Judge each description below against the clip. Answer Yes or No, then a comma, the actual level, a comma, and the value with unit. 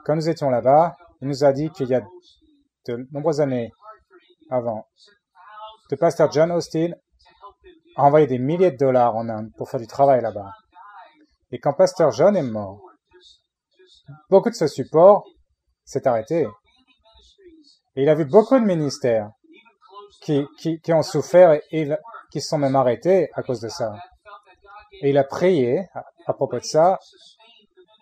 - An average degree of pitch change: No, wide, 7.1 semitones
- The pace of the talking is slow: No, average, 165 wpm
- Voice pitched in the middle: Yes, medium, 160 Hz